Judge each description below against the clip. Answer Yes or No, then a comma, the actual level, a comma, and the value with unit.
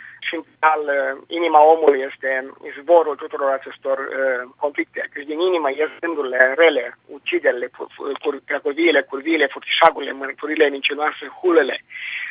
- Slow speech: Yes, slow, 110 wpm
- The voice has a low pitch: No, medium, 170 Hz